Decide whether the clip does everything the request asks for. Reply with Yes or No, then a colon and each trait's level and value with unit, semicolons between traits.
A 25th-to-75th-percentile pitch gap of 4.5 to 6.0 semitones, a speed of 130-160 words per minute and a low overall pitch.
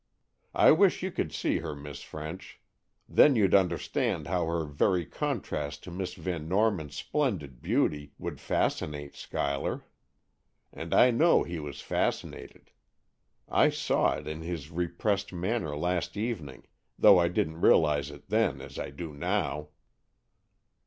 Yes: average, 5.0 semitones; average, 140 wpm; very low, 85 Hz